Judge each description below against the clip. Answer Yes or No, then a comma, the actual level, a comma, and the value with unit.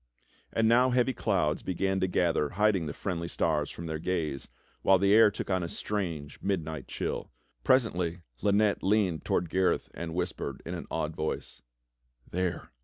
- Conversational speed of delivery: Yes, average, 170 wpm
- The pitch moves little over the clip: No, average, 3.7 semitones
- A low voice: Yes, very low, 90 Hz